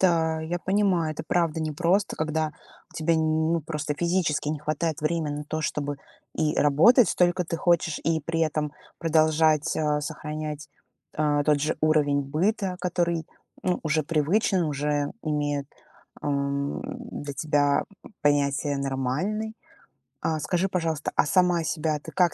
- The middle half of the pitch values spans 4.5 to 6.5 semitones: No, narrow, 2.6 semitones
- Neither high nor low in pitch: Yes, medium, 155 Hz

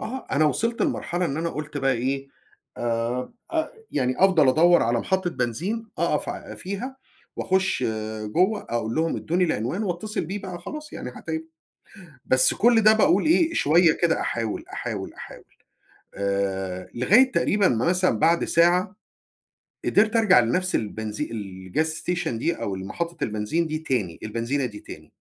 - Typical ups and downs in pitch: No, wide, 8.1 semitones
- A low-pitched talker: No, medium, 160 Hz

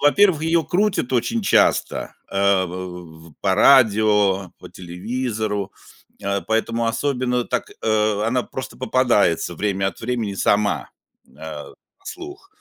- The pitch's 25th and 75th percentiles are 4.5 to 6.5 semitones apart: Yes, average, 4.9 semitones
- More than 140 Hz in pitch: No, low, 110 Hz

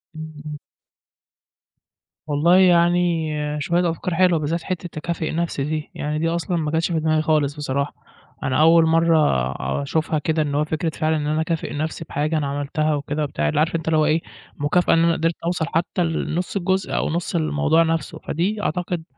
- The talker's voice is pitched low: No, medium, 160 Hz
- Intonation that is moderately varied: No, narrow, 1.9 semitones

